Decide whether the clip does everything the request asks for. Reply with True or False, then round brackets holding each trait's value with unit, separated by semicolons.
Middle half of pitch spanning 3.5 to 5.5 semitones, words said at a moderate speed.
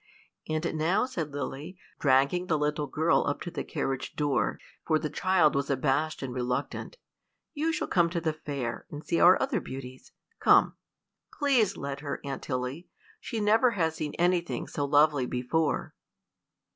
True (4.1 semitones; 160 wpm)